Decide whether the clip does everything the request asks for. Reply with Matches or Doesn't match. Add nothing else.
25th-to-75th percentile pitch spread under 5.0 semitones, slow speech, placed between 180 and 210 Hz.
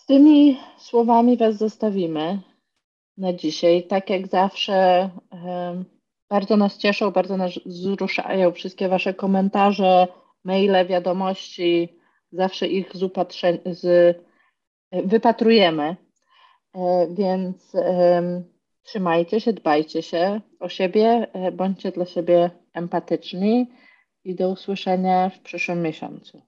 Matches